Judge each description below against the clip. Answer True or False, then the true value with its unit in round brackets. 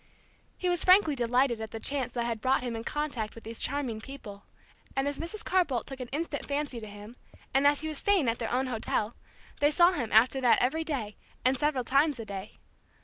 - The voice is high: True (260 Hz)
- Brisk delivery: True (225 wpm)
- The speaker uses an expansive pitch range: False (4.3 semitones)